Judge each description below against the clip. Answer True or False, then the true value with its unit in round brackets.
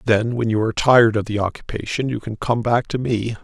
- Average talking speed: False (245 wpm)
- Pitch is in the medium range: False (115 Hz)